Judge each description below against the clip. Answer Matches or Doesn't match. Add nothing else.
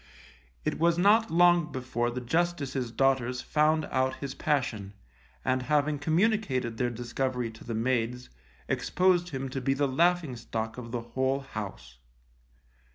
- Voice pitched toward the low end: Matches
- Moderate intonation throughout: Matches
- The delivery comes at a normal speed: Matches